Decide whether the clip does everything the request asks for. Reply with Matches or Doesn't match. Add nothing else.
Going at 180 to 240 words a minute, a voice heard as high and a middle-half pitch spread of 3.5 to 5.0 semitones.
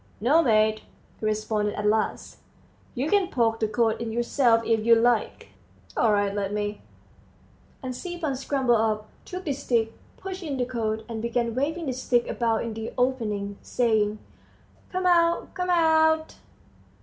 Doesn't match